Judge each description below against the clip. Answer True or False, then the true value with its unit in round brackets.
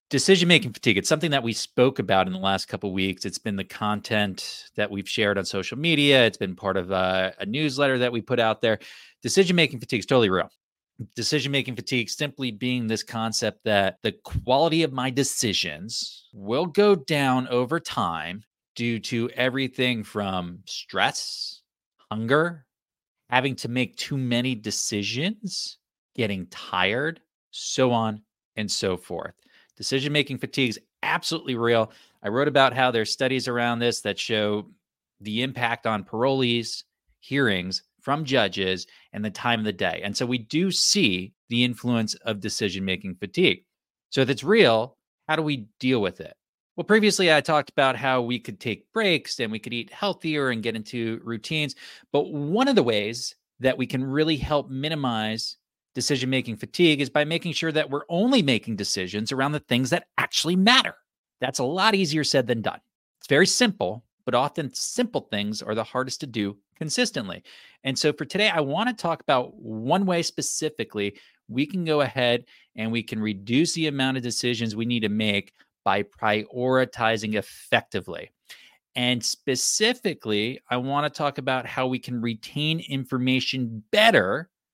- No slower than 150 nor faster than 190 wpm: True (170 wpm)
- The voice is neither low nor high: False (125 Hz)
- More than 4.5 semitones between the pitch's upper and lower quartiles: True (5.1 semitones)